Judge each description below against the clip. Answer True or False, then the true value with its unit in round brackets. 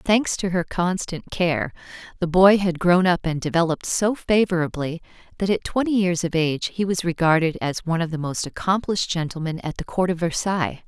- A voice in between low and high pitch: True (175 Hz)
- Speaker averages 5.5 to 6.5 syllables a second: True (5.6 syllables/s)